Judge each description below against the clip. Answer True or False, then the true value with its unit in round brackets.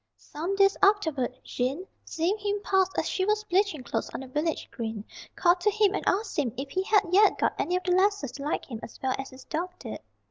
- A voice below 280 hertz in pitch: False (360 Hz)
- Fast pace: True (235 wpm)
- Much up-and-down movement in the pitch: True (6.6 semitones)